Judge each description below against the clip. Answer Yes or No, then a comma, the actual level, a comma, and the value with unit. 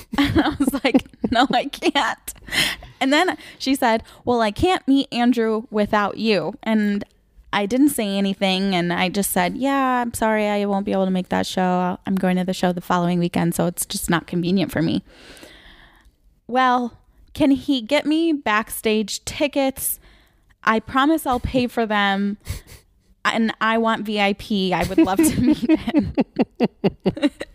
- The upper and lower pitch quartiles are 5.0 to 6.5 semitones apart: Yes, wide, 5.4 semitones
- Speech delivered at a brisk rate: No, average, 165 wpm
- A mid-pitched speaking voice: No, high, 220 Hz